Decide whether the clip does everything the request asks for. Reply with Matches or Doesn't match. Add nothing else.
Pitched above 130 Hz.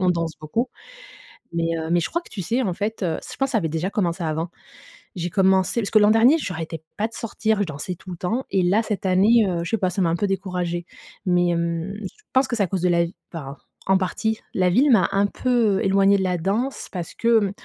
Matches